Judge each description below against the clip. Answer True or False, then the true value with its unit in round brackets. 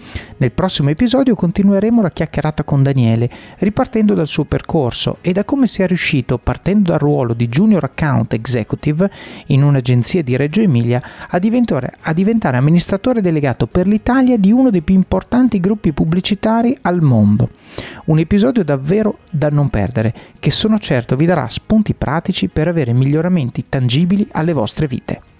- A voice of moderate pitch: True (165 Hz)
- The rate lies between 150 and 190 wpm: True (155 wpm)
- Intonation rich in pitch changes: True (6.8 semitones)